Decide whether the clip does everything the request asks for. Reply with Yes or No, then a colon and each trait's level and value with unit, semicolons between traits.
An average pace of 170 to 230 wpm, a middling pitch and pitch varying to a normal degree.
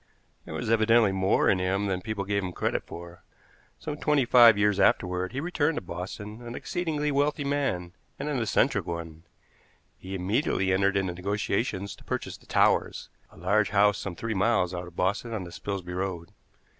No: average, 180 wpm; low, 100 Hz; average, 4.3 semitones